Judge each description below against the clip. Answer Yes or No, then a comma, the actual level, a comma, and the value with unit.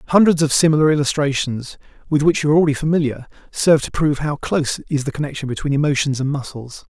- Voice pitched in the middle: Yes, medium, 145 Hz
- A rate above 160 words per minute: Yes, average, 190 wpm